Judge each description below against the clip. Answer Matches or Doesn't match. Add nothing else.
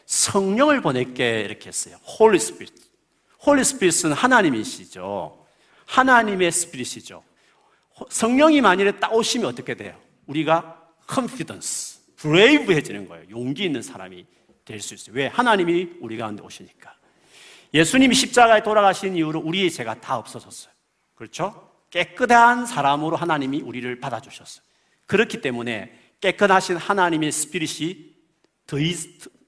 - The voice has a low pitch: Doesn't match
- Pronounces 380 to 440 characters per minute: Matches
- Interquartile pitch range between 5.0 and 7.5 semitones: Doesn't match